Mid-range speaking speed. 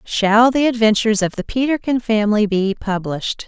Yes: average, 155 wpm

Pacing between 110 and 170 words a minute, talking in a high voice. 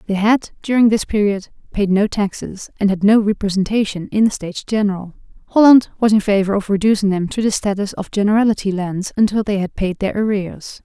No: average, 195 wpm; high, 205 Hz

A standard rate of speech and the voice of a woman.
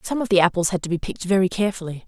No: fast, 290 wpm; female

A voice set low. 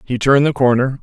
Yes: low, 130 Hz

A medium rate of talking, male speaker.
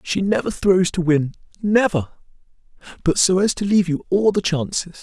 Yes: average, 155 wpm; male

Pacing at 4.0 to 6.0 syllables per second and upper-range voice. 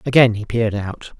No: 5.8 syllables/s; low, 115 Hz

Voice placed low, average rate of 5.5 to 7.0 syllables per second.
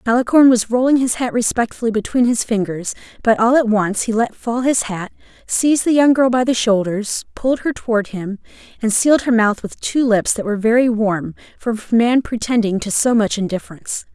No: high, 230 Hz; 5.6 syllables/s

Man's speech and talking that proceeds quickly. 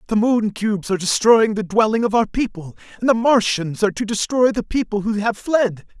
Yes: male; fast, 210 wpm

